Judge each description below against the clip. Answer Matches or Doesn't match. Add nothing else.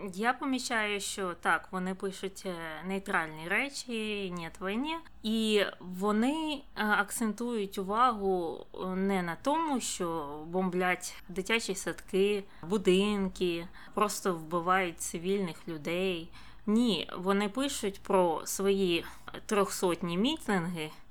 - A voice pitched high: Matches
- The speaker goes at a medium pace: Doesn't match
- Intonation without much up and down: Doesn't match